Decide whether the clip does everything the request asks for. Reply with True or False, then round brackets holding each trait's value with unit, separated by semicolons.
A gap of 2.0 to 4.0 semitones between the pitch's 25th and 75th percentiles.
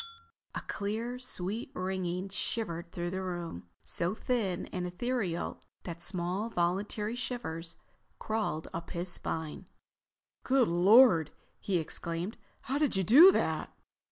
False (4.6 semitones)